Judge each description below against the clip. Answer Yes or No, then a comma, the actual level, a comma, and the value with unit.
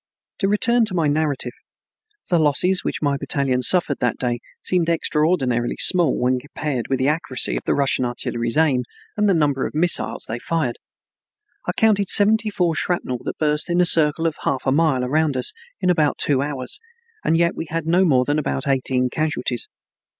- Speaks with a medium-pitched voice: Yes, medium, 150 Hz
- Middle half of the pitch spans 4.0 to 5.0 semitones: Yes, average, 4.7 semitones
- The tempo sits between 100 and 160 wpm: No, average, 185 wpm